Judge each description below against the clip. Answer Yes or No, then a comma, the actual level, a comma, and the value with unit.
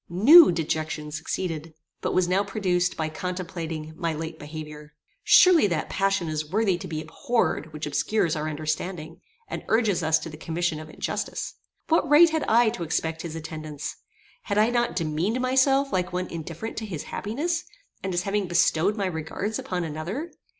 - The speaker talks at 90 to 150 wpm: No, average, 170 wpm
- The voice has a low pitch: No, medium, 175 Hz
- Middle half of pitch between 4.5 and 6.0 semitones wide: Yes, average, 5.0 semitones